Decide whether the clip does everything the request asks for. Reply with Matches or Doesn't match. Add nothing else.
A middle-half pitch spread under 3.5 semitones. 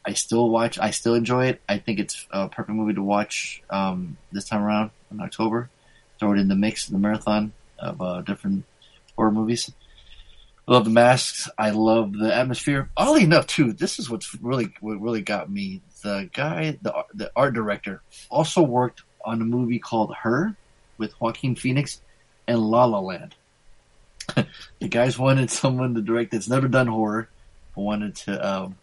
Matches